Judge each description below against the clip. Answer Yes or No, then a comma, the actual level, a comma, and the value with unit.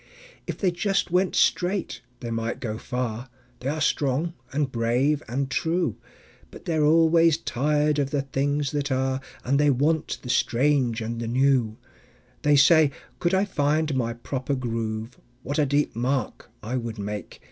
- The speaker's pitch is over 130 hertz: Yes, medium, 140 Hz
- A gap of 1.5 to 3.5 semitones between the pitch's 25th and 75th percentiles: No, average, 4.1 semitones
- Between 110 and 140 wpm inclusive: No, average, 160 wpm